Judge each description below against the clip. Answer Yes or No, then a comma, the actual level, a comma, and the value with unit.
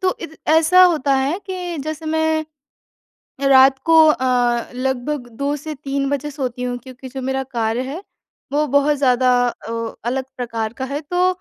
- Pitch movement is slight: No, average, 3.6 semitones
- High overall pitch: Yes, very high, 275 Hz